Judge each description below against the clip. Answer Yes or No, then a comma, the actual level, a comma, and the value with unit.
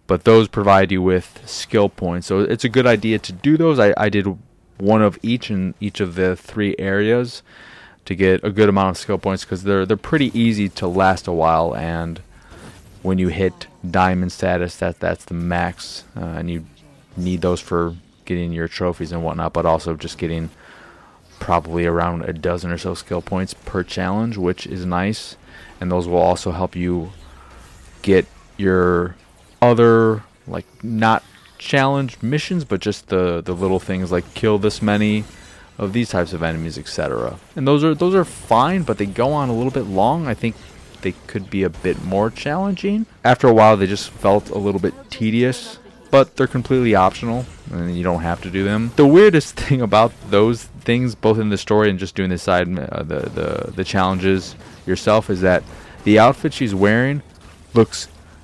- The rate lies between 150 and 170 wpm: No, average, 190 wpm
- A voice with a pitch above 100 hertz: No, very low, 95 Hz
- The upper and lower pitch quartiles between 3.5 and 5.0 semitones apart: Yes, average, 4.1 semitones